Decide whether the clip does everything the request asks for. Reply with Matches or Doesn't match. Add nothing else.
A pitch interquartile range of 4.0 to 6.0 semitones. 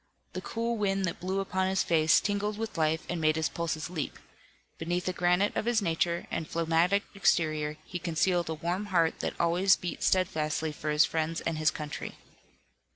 Doesn't match